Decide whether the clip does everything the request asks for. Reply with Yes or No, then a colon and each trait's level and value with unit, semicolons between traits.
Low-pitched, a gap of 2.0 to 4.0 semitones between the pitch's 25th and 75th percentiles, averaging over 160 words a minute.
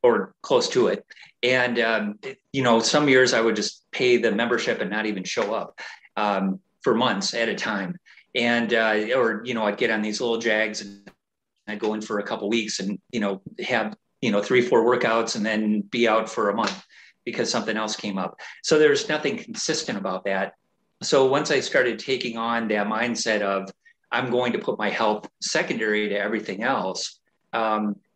Yes: low, 115 Hz; average, 2.7 semitones; average, 200 wpm